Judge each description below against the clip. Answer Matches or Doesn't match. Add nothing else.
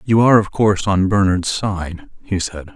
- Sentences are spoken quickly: Doesn't match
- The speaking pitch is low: Matches